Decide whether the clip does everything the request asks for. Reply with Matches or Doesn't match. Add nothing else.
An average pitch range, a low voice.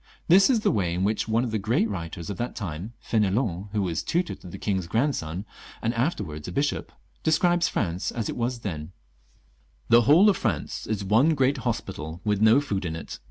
Doesn't match